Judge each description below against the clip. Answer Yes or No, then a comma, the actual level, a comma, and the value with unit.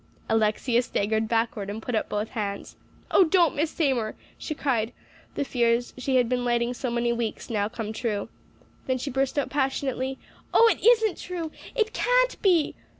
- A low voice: No, high, 245 Hz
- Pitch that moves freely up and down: No, average, 4.4 semitones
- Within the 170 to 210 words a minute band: Yes, average, 175 wpm